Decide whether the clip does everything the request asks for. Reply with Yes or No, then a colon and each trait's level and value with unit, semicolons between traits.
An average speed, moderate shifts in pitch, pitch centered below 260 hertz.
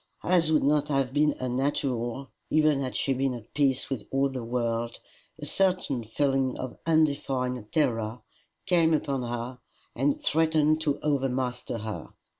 Yes: average, 145 wpm; average, 3.2 semitones; low, 135 Hz